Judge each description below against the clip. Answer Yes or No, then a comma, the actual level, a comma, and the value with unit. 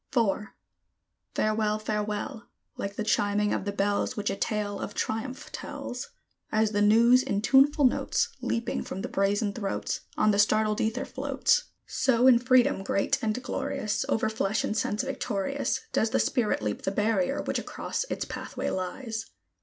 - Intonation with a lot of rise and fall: No, narrow, 2.4 semitones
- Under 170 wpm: Yes, average, 160 wpm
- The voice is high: Yes, high, 215 Hz